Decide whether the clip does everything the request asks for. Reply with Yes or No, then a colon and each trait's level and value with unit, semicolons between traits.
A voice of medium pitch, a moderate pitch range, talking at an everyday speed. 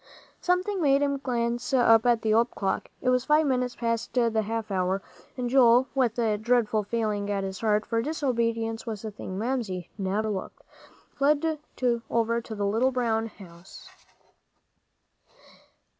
No: high, 230 Hz; average, 3.0 semitones; average, 155 wpm